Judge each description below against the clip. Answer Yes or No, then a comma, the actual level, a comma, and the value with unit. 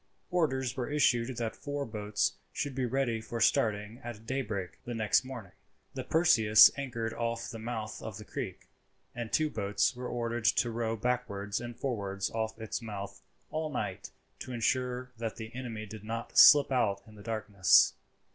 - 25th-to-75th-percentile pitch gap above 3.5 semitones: No, average, 2.7 semitones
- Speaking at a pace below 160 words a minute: No, average, 170 wpm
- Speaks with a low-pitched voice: Yes, low, 115 Hz